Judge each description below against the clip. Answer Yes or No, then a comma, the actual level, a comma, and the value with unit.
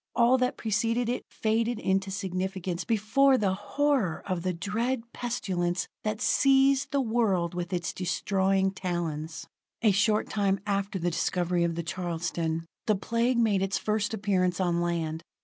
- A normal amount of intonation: Yes, average, 4.5 semitones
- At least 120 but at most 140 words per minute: No, average, 150 wpm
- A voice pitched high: Yes, high, 195 Hz